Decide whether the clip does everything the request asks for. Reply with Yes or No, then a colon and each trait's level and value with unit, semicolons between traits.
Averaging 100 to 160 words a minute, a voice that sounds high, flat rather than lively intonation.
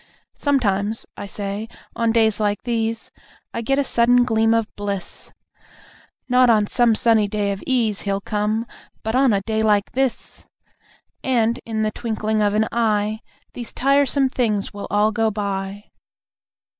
Yes: average, 155 wpm; high, 220 Hz; narrow, 2.3 semitones